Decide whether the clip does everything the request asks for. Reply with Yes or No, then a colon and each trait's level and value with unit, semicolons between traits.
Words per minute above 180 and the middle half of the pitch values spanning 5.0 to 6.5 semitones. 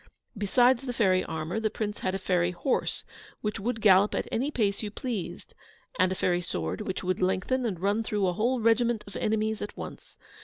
No: average, 200 wpm; average, 3.5 semitones